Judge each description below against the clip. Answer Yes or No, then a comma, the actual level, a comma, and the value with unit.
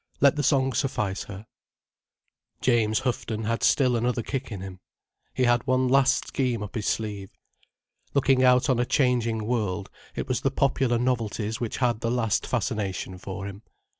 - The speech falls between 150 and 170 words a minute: Yes, average, 165 wpm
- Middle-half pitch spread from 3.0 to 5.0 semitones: Yes, average, 3.3 semitones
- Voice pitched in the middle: No, low, 120 Hz